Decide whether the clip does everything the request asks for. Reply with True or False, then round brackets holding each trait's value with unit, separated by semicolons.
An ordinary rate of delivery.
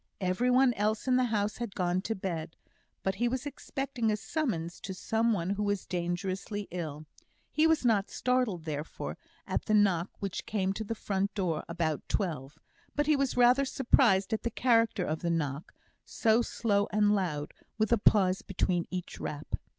True (180 wpm)